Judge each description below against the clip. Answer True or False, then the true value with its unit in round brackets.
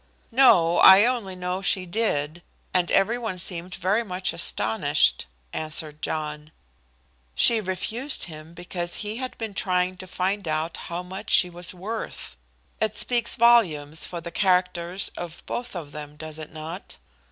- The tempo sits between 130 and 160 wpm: True (150 wpm)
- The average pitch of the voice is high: False (180 Hz)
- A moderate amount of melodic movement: True (4.1 semitones)